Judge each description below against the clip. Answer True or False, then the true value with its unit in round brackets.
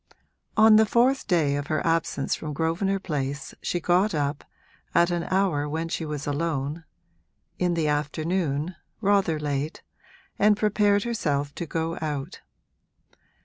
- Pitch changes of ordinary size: True (4.5 semitones)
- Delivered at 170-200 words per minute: False (140 wpm)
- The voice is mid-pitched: True (165 Hz)